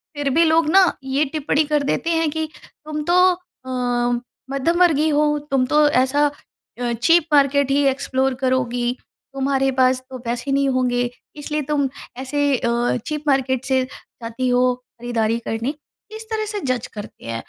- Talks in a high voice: Yes, very high, 270 Hz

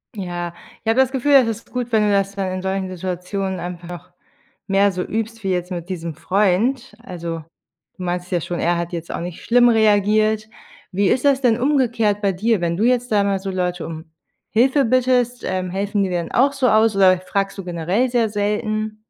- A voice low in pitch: No, high, 200 Hz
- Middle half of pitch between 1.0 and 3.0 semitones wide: No, average, 4.0 semitones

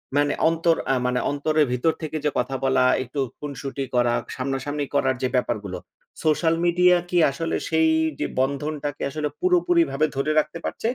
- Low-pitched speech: No, medium, 145 Hz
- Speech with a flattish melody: No, average, 3.3 semitones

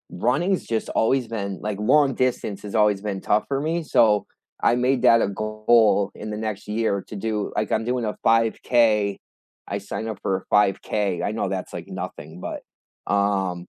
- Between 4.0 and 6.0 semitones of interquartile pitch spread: No, narrow, 2.5 semitones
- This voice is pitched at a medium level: No, low, 105 Hz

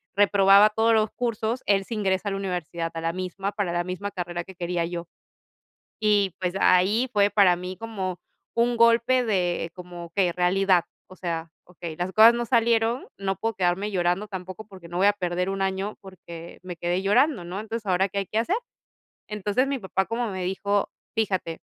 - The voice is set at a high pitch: Yes, high, 195 Hz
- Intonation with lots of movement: No, average, 3.2 semitones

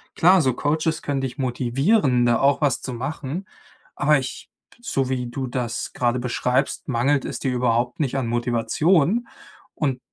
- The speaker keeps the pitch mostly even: No, average, 3.2 semitones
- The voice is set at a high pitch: No, low, 130 Hz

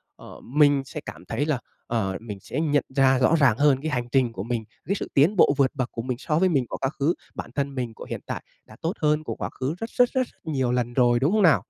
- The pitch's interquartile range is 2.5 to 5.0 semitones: Yes, average, 3.9 semitones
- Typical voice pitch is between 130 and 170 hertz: Yes, low, 135 Hz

